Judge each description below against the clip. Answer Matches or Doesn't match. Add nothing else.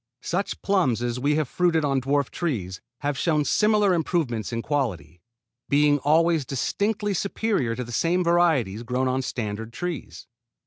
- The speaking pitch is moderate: Matches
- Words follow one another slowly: Doesn't match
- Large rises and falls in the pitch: Matches